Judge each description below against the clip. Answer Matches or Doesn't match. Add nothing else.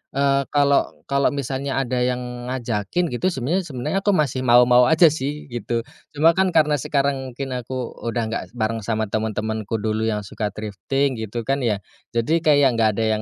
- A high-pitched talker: Doesn't match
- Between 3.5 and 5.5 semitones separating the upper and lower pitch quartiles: Matches